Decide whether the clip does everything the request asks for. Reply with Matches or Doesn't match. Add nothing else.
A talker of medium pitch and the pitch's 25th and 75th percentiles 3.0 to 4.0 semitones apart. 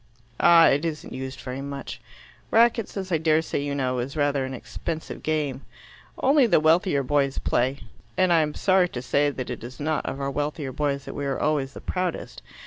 Matches